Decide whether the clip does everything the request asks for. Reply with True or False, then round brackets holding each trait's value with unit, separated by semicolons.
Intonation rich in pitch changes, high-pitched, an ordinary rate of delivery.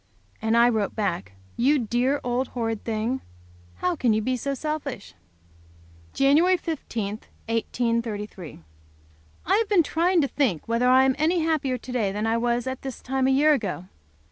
False (3.8 semitones; 245 Hz; 170 wpm)